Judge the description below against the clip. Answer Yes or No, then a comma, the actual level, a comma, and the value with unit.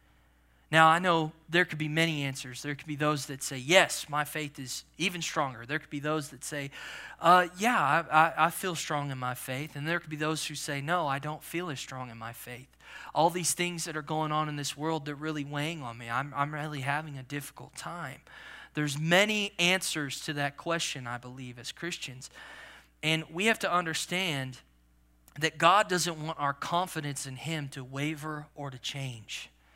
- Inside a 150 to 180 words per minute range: No, fast, 205 wpm